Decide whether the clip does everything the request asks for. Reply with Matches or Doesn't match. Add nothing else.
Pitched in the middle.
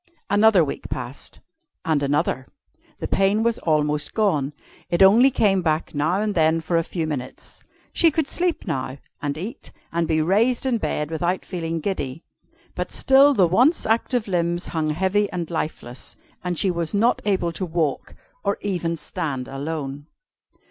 Matches